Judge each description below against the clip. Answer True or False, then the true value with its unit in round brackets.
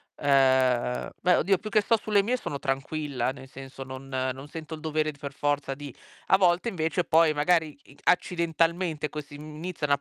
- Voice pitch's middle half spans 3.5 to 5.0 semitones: True (3.9 semitones)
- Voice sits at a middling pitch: True (150 Hz)